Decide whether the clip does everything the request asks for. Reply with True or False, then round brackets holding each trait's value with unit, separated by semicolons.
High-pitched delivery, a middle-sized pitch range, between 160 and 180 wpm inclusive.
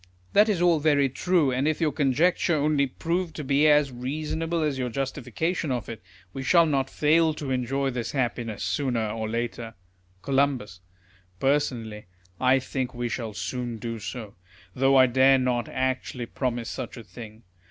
False (135 Hz; 3.7 semitones; 165 wpm)